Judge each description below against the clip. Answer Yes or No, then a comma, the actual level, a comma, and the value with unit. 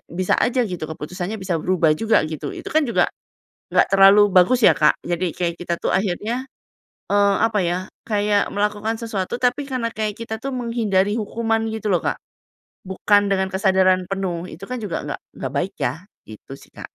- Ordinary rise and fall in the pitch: Yes, average, 3.6 semitones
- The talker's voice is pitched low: No, high, 200 Hz